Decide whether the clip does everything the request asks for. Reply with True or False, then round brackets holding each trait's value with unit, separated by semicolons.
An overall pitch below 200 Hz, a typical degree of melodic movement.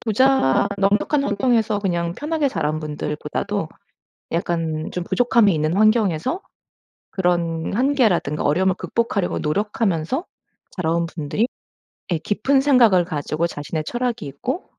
False (190 Hz; 6.4 semitones)